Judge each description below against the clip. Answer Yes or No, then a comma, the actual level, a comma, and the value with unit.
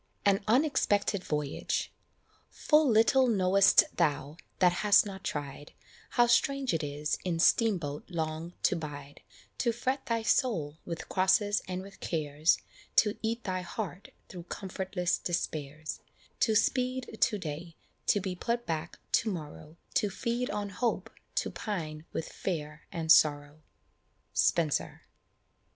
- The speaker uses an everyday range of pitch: No, wide, 5.9 semitones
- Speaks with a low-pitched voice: No, medium, 185 Hz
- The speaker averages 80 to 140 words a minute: Yes, slow, 135 wpm